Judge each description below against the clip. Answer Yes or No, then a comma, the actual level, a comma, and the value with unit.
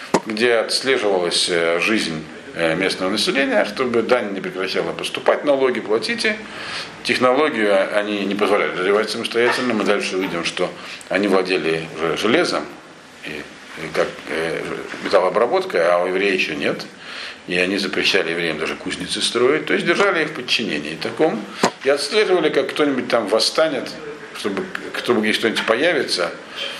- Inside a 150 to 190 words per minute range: No, average, 130 wpm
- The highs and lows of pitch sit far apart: Yes, wide, 7.0 semitones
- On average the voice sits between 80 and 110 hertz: Yes, low, 100 Hz